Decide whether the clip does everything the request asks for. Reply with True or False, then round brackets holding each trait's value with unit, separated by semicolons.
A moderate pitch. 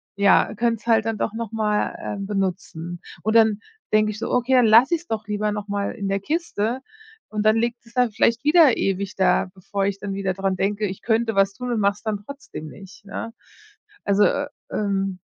False (210 Hz)